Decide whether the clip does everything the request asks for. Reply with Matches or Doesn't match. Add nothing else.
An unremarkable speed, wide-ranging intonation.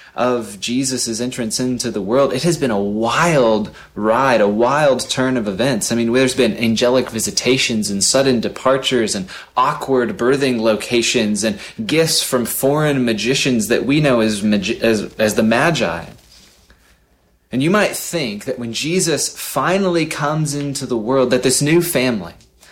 Doesn't match